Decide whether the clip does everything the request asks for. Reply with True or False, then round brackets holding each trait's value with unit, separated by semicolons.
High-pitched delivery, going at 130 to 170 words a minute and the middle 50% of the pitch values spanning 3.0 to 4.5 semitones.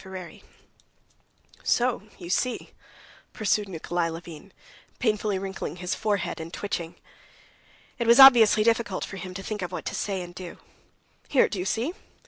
True (195 Hz; 155 wpm; 3.5 semitones)